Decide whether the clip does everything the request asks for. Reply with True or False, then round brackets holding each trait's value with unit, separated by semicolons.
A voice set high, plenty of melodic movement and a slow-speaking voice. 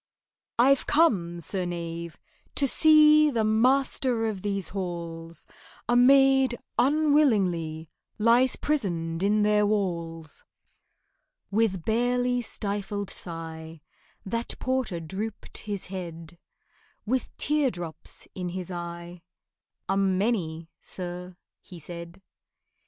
True (195 Hz; 6.1 semitones; 100 wpm)